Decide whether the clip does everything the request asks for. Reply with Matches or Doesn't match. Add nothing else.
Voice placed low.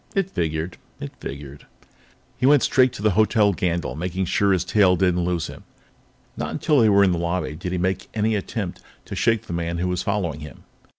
Matches